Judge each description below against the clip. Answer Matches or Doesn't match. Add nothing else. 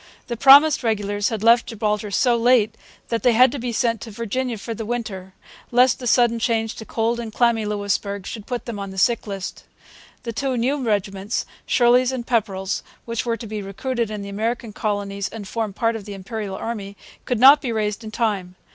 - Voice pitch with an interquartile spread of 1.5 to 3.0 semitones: Matches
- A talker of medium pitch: Doesn't match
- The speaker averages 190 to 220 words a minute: Matches